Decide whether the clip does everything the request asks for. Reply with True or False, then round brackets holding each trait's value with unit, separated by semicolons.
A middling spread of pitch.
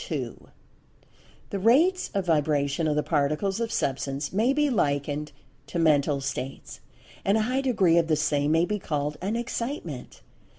False (7.1 semitones)